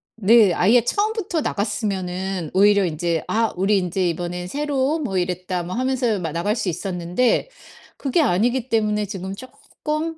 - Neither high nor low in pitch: No, high, 205 Hz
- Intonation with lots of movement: Yes, wide, 6.1 semitones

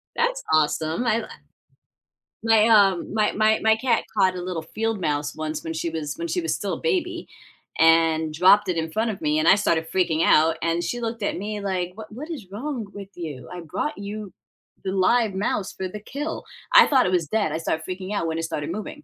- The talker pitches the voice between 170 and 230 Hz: Yes, high, 190 Hz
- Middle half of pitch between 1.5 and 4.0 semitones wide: No, average, 5.1 semitones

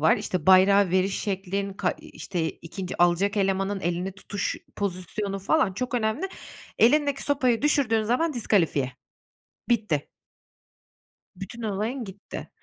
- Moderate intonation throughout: Yes, average, 3.8 semitones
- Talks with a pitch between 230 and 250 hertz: No, high, 200 Hz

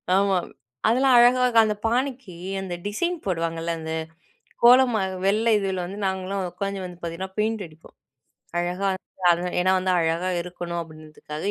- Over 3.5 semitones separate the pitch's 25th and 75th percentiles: Yes, average, 4.0 semitones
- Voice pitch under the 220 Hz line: Yes, high, 190 Hz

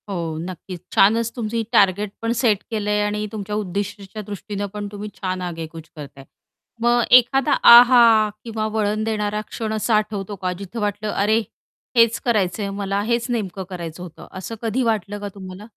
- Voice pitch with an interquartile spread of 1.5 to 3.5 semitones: Yes, narrow, 2.6 semitones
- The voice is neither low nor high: No, high, 210 Hz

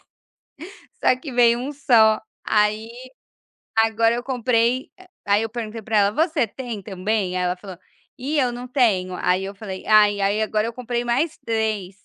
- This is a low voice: No, high, 225 Hz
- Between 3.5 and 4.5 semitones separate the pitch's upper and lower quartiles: No, average, 3.1 semitones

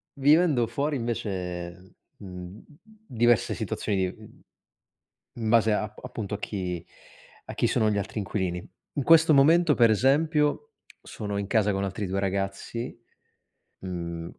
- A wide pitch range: Yes, wide, 6.2 semitones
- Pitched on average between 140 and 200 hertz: No, low, 105 Hz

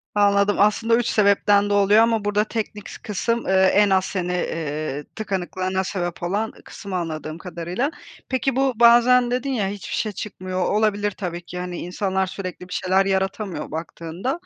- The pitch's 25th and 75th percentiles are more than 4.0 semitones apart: No, average, 2.9 semitones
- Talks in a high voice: Yes, high, 195 Hz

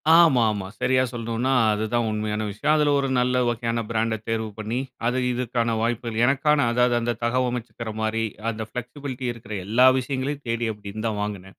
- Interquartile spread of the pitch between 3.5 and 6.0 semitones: No, narrow, 2.5 semitones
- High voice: No, low, 120 Hz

